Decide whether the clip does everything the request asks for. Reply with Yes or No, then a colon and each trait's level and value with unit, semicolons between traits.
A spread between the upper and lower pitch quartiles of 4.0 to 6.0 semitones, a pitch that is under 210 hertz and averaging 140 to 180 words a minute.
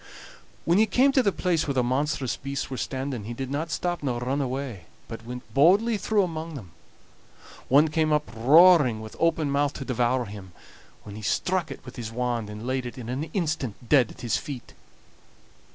No: average, 4.9 semitones; low, 135 Hz; average, 200 wpm